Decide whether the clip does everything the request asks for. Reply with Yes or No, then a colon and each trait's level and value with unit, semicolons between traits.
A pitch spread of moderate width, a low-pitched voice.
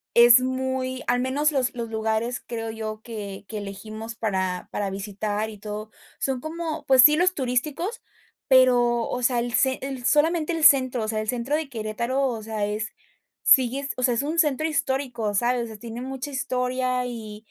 No: average, 3.4 semitones; high, 245 Hz